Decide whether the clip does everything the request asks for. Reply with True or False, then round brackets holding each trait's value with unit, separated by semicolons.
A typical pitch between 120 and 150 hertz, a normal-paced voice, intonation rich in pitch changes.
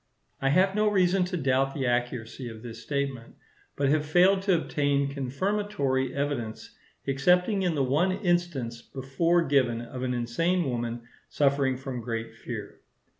True (140 Hz; 150 wpm; 5.8 semitones)